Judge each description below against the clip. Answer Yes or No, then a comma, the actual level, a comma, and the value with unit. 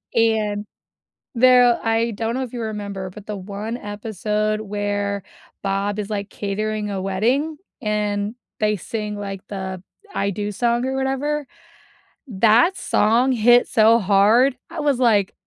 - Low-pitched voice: No, high, 215 Hz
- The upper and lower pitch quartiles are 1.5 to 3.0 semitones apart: Yes, average, 2.7 semitones